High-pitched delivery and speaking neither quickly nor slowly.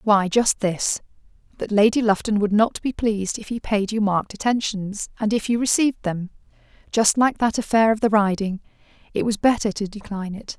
Yes: high, 210 Hz; average, 185 wpm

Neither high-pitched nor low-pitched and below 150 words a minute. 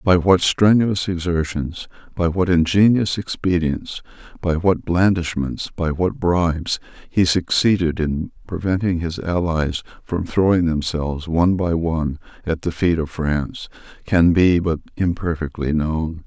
No: very low, 85 Hz; slow, 135 wpm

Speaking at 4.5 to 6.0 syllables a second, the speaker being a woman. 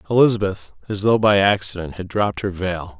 No: 5.7 syllables/s; male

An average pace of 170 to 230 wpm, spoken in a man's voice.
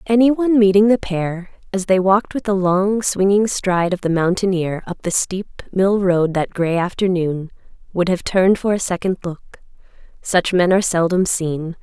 No: average, 180 wpm; female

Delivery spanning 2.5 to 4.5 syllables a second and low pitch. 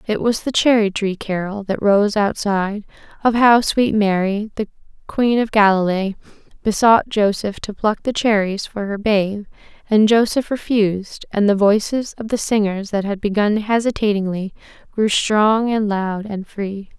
No: 4.4 syllables/s; high, 210 Hz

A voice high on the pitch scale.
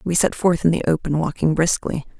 No: medium, 165 Hz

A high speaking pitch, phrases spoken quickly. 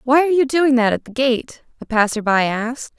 Yes: very high, 250 Hz; fast, 240 wpm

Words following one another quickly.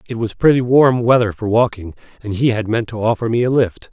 Yes: fast, 245 wpm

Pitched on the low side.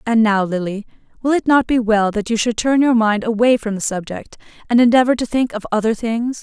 No: high, 225 Hz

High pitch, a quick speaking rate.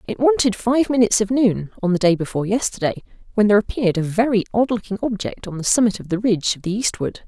Yes: high, 210 Hz; fast, 230 wpm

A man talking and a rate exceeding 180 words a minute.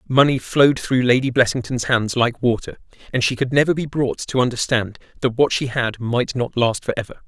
Yes: male; fast, 205 wpm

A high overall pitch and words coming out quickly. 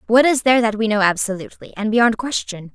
Yes: high, 225 Hz; fast, 220 wpm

